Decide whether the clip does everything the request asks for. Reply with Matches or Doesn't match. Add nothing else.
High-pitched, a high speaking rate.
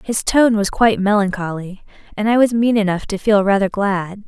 Doesn't match